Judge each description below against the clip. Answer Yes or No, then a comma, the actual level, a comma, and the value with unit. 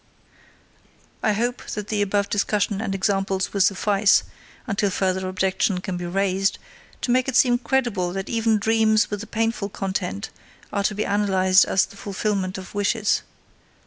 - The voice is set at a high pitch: Yes, high, 200 Hz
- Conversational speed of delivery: Yes, average, 160 wpm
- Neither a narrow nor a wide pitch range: No, narrow, 2.1 semitones